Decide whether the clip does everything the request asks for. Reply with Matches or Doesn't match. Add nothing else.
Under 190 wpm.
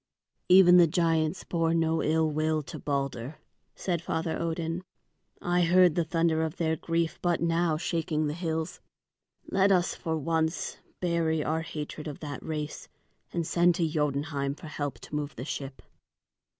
Matches